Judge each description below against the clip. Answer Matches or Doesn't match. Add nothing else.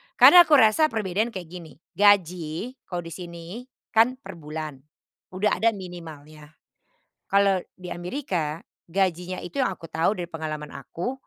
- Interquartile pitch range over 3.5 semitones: Matches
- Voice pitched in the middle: Matches